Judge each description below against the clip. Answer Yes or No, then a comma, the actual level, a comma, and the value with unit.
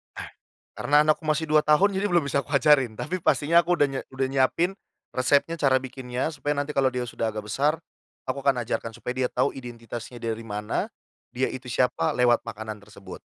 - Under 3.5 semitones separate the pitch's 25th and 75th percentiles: No, average, 3.8 semitones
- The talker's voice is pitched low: Yes, low, 130 Hz